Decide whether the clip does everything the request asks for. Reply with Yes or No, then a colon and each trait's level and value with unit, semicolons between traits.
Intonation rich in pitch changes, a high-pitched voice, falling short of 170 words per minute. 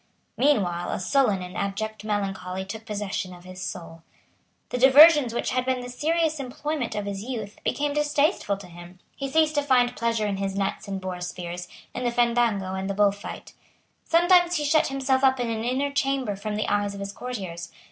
No: wide, 5.7 semitones; high, 220 Hz; average, 195 wpm